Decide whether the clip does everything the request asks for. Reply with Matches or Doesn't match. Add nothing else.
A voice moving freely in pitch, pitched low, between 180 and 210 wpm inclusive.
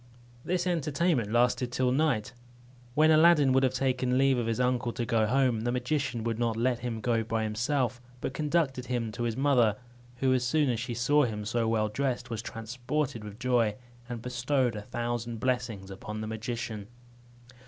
Doesn't match